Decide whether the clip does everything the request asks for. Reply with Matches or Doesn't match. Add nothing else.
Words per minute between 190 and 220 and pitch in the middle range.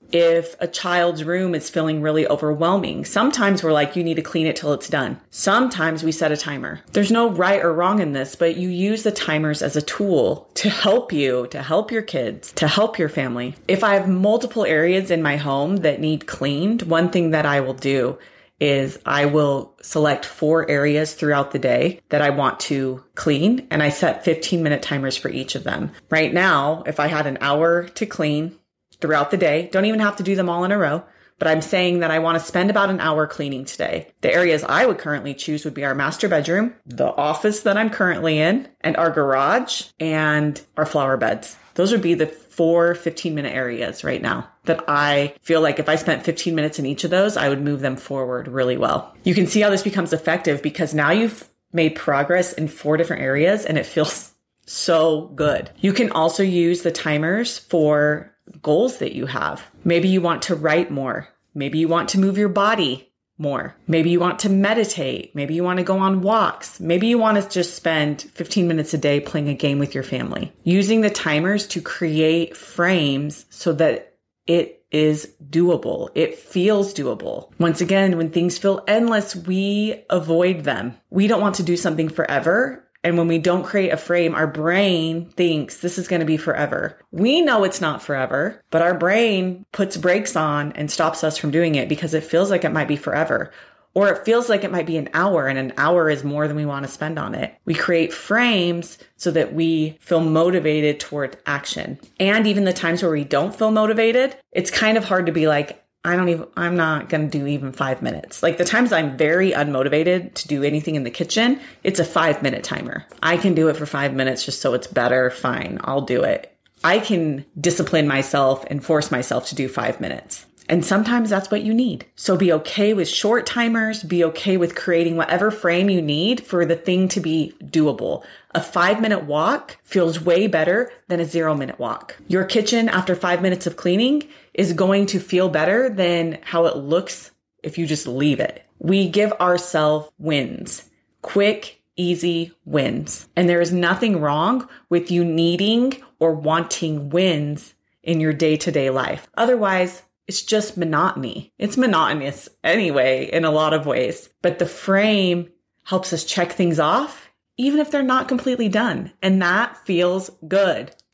Matches